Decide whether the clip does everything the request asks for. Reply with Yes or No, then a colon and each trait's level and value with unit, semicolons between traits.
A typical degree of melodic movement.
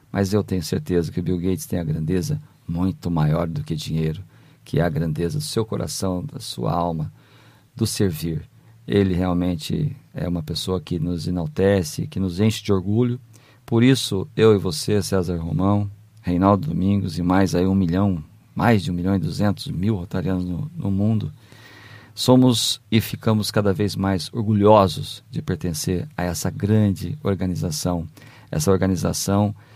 Yes: average, 3.7 semitones